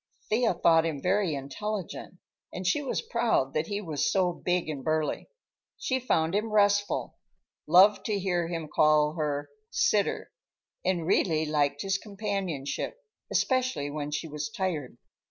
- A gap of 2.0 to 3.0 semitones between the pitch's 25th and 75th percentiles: No, average, 5.0 semitones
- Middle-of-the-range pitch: Yes, medium, 175 Hz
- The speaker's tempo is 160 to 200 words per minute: No, average, 145 wpm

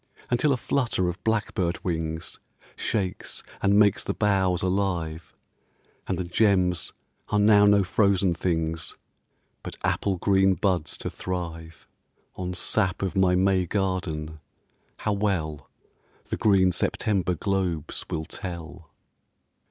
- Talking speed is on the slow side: Yes, slow, 120 wpm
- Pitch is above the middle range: No, very low, 95 Hz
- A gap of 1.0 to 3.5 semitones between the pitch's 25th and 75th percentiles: Yes, average, 2.7 semitones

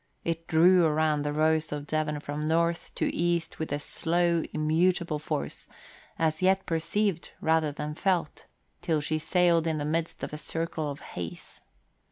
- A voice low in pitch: No, medium, 160 Hz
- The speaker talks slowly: No, average, 165 wpm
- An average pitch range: No, narrow, 1.8 semitones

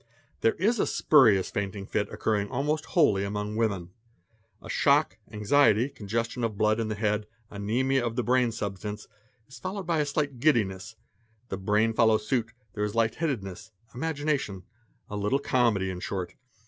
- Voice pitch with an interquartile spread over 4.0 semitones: Yes, average, 4.4 semitones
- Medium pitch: No, low, 110 Hz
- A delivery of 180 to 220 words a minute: No, average, 165 wpm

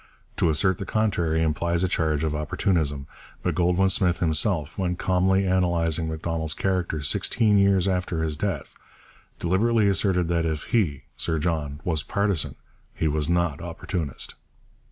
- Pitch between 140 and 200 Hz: No, very low, 85 Hz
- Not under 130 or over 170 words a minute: Yes, average, 145 wpm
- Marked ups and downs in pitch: No, average, 3.0 semitones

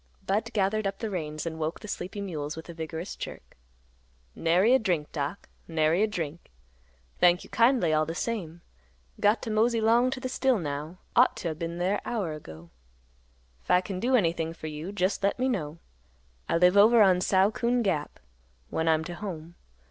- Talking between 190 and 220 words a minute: Yes, average, 195 wpm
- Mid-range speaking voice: Yes, medium, 180 Hz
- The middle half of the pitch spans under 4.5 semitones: No, average, 5.0 semitones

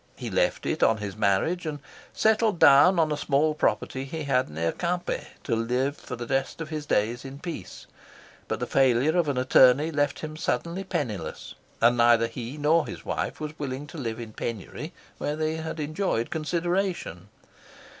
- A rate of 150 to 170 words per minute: No, average, 180 wpm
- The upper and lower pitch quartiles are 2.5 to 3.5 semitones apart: No, average, 5.0 semitones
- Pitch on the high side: No, medium, 145 Hz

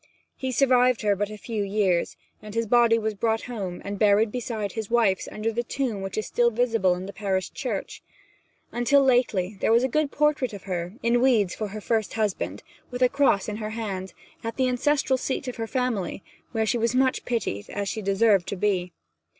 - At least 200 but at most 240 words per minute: Yes, fast, 205 wpm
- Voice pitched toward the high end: Yes, high, 220 Hz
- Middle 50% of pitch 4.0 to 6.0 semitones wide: No, average, 3.6 semitones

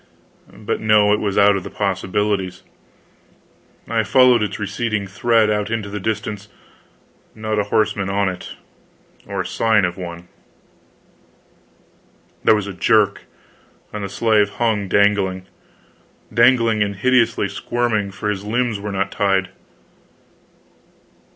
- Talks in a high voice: No, low, 105 Hz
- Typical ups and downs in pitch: No, narrow, 1.9 semitones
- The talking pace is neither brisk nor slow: No, slow, 125 wpm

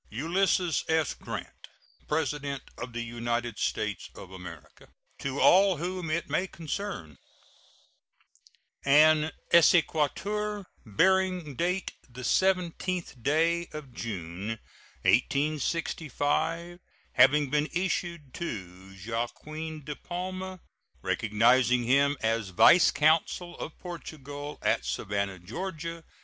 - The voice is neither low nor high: Yes, medium, 150 Hz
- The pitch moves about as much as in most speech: No, wide, 6.4 semitones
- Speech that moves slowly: Yes, slow, 100 wpm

